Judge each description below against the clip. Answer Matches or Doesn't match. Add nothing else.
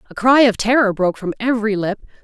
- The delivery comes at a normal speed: Doesn't match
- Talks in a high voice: Matches